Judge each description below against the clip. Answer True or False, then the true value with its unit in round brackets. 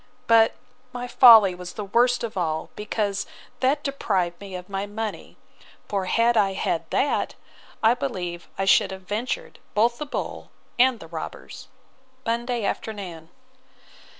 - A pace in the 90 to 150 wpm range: True (145 wpm)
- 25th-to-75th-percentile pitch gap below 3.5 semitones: False (4.3 semitones)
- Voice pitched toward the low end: False (210 Hz)